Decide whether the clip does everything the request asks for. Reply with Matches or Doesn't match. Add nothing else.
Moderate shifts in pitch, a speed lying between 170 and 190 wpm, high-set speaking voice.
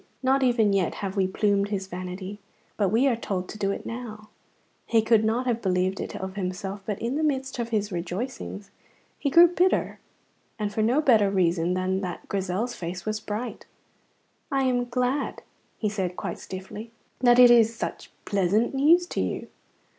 Matches